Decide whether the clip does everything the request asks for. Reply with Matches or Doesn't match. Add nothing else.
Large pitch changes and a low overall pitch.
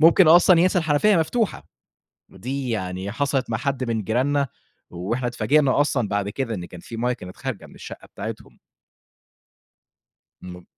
Matches